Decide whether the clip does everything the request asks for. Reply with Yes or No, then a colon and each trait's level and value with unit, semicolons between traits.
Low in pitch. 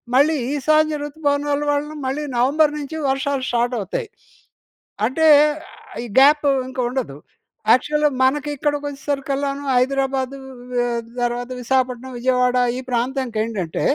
No: very high, 270 Hz